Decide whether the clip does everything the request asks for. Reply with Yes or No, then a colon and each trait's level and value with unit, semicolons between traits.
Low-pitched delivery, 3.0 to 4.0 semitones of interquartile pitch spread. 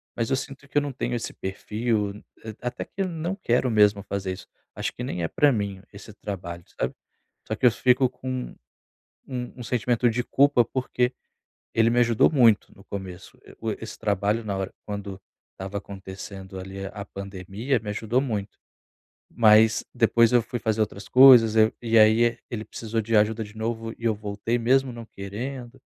Yes: low, 110 Hz; average, 3.3 semitones